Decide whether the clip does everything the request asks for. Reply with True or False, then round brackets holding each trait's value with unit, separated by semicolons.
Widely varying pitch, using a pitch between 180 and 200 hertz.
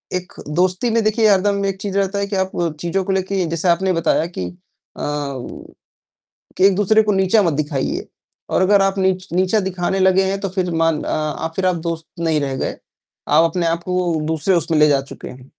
False (3.0 semitones; 185 Hz)